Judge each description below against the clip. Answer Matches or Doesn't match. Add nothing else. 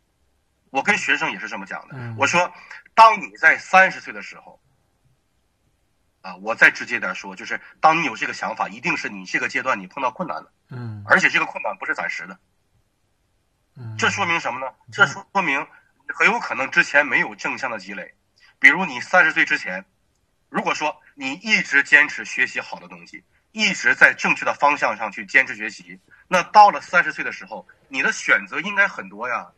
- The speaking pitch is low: Doesn't match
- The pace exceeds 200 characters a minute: Matches